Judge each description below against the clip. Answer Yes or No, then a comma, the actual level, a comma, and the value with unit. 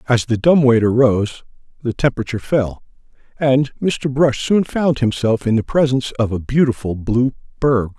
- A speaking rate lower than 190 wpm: Yes, average, 165 wpm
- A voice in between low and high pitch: No, low, 125 Hz